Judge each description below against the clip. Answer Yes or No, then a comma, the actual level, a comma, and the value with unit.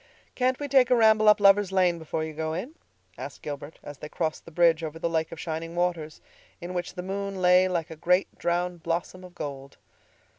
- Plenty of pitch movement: No, average, 3.0 semitones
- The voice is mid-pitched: Yes, medium, 175 Hz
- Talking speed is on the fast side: Yes, fast, 215 wpm